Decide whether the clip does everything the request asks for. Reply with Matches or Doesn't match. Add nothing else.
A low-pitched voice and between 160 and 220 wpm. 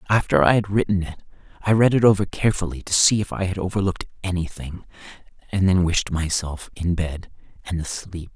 Matches